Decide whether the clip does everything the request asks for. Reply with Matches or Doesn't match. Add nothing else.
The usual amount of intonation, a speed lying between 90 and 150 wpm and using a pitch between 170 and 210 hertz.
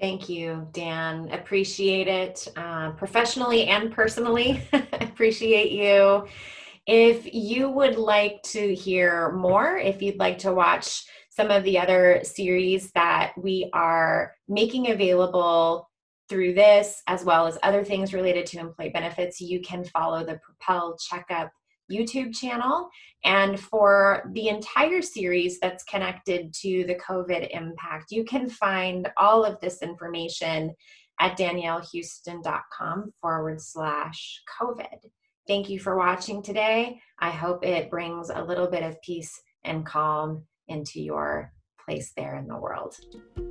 Matches